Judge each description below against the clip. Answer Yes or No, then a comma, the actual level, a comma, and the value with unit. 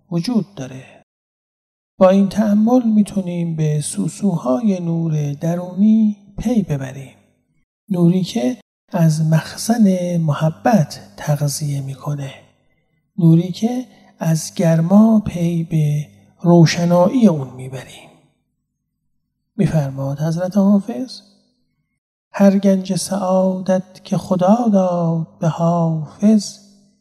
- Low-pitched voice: No, medium, 180 Hz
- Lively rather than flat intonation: No, average, 4.3 semitones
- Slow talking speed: Yes, slow, 85 wpm